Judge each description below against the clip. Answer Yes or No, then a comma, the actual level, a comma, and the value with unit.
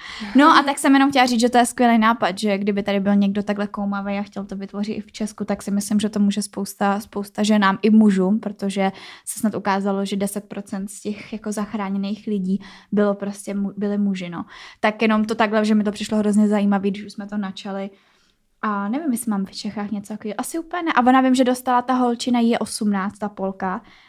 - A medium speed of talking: No, fast, 225 wpm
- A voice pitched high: Yes, high, 210 Hz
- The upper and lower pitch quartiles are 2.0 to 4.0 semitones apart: No, narrow, 1.6 semitones